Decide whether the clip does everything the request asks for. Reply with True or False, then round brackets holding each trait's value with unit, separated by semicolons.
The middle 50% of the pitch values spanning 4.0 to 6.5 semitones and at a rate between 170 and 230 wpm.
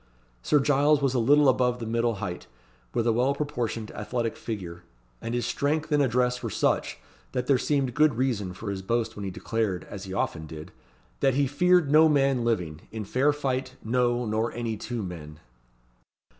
True (4.4 semitones; 185 wpm)